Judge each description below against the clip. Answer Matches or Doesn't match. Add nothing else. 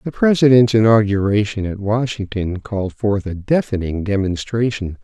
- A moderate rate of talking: Doesn't match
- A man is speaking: Matches